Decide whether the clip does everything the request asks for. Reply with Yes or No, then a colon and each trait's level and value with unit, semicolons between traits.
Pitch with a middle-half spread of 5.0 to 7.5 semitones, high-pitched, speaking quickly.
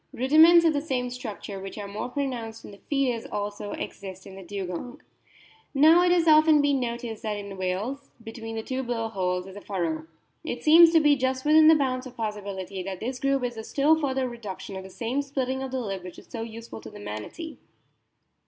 Yes: wide, 5.5 semitones; high, 240 Hz; fast, 220 wpm